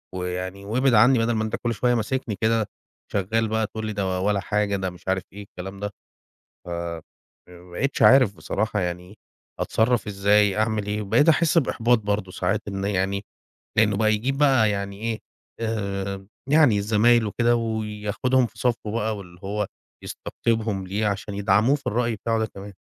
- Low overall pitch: Yes, low, 105 Hz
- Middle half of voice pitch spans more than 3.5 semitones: No, narrow, 2.6 semitones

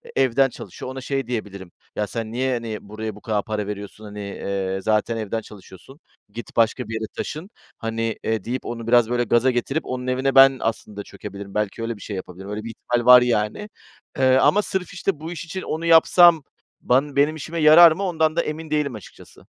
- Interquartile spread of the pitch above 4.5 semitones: Yes, average, 4.9 semitones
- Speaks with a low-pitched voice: Yes, low, 120 Hz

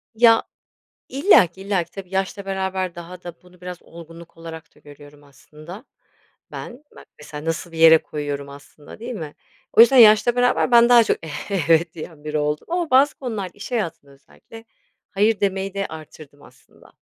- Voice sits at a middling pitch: Yes, medium, 180 Hz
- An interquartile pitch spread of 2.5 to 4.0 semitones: No, wide, 5.5 semitones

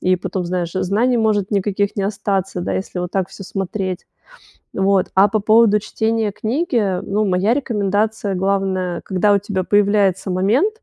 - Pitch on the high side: Yes, high, 200 Hz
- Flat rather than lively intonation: Yes, narrow, 2.2 semitones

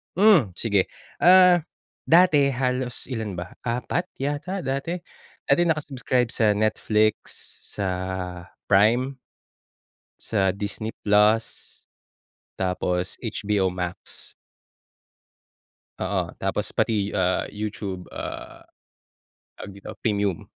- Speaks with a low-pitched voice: Yes, low, 110 Hz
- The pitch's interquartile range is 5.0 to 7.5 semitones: Yes, average, 5.3 semitones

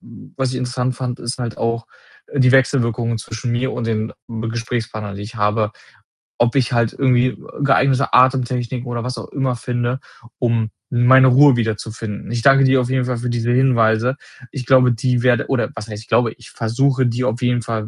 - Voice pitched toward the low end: Yes, low, 120 Hz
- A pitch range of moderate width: No, narrow, 2.0 semitones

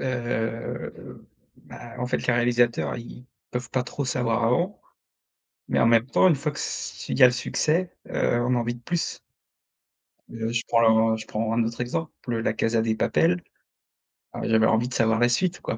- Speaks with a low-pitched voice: Yes, low, 120 Hz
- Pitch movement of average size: No, narrow, 2.0 semitones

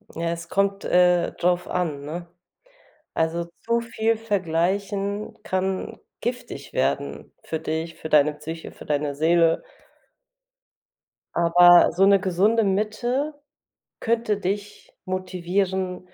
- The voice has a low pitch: No, medium, 185 Hz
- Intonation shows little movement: No, average, 3.3 semitones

